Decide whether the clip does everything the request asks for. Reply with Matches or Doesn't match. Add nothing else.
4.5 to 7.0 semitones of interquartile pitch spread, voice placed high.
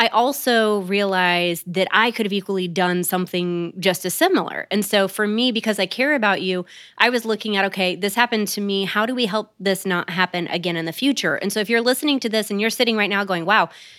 Doesn't match